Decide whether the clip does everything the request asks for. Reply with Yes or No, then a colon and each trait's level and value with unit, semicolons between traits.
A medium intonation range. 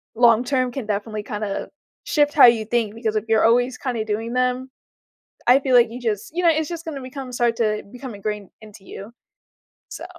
Yes: average, 3.1 semitones